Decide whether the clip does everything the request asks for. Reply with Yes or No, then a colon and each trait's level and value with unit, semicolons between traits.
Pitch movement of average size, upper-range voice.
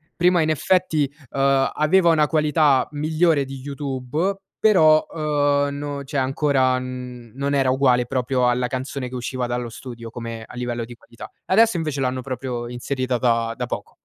No: average, 3.3 semitones; low, 135 Hz